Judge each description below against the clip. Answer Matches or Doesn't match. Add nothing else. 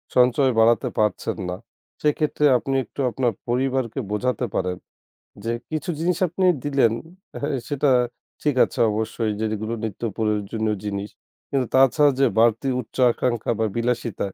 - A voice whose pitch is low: Matches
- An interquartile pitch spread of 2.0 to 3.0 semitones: Doesn't match